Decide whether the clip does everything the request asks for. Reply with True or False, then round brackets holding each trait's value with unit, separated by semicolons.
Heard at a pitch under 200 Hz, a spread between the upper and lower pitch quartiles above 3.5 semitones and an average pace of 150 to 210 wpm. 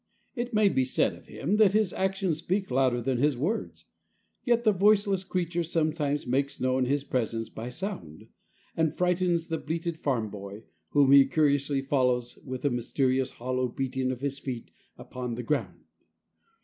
True (140 Hz; 5.6 semitones; 165 wpm)